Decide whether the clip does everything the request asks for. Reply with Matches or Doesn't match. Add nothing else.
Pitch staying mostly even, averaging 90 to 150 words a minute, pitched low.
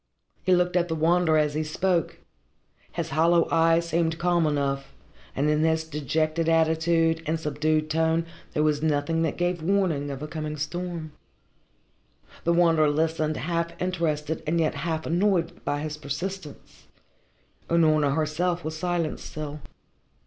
Doesn't match